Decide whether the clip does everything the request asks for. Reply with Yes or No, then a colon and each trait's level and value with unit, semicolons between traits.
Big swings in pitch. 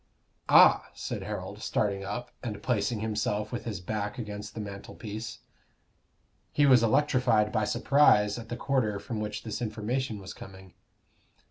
No: narrow, 2.6 semitones